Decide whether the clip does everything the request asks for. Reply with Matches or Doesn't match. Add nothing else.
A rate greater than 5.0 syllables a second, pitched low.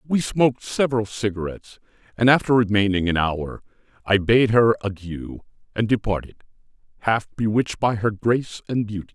Matches